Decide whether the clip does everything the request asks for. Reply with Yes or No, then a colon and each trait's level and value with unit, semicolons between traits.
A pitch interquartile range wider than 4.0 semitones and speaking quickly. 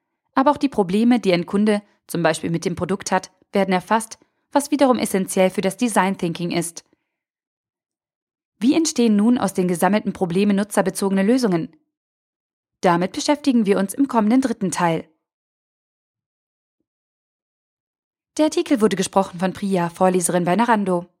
No: average, 4.9 semitones; average, 140 wpm